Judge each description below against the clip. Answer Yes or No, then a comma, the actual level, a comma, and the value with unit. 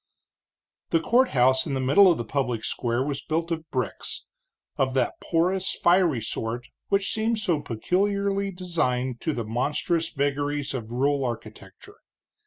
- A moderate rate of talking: Yes, average, 145 wpm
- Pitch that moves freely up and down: Yes, wide, 6.0 semitones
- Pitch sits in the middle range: Yes, medium, 145 Hz